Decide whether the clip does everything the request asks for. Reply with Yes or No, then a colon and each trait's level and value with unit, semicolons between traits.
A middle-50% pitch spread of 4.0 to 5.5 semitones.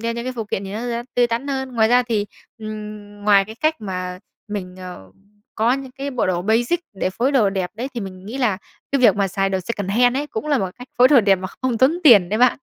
Yes: average, 4.3 semitones